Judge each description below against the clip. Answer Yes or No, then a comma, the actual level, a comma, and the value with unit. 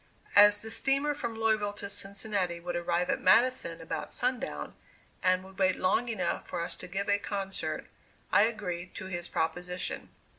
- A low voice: No, high, 195 Hz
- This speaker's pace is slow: No, average, 170 wpm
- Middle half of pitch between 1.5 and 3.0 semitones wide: No, average, 3.6 semitones